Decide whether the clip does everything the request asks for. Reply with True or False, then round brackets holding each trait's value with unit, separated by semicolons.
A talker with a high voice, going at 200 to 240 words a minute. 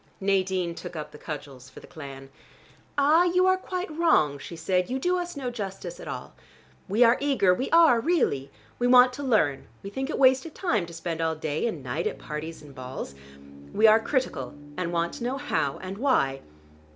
True (195 Hz; 205 wpm)